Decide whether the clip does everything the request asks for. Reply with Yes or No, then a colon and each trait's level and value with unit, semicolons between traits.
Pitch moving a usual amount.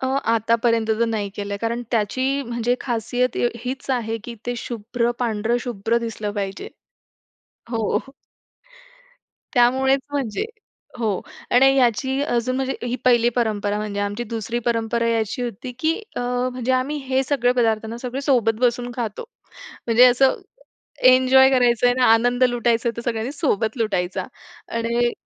No: narrow, 2.1 semitones